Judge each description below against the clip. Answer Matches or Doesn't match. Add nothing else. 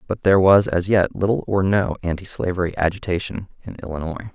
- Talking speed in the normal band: Matches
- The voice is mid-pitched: Doesn't match